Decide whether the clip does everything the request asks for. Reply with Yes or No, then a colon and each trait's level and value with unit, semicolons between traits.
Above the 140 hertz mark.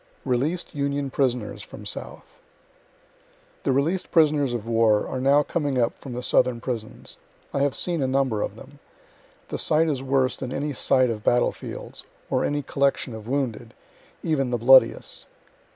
No: low, 135 Hz